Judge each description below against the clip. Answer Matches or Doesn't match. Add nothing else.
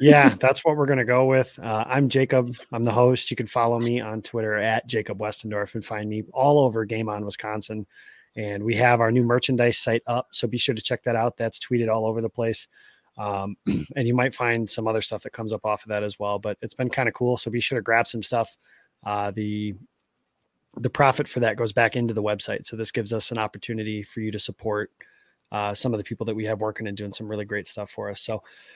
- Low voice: Matches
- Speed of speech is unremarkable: Doesn't match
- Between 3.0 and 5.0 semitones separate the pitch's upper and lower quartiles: Doesn't match